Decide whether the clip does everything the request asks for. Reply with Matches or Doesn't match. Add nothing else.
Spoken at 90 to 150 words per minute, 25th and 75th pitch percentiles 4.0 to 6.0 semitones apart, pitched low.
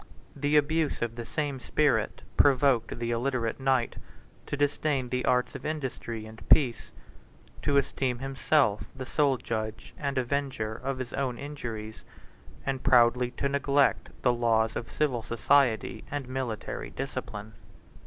Doesn't match